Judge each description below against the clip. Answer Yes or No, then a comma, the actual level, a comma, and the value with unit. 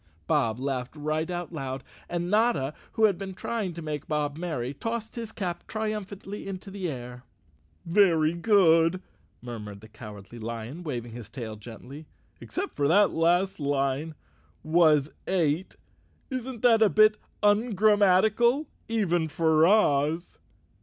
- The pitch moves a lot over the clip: Yes, wide, 6.5 semitones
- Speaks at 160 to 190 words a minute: No, average, 140 wpm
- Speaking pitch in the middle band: Yes, medium, 165 Hz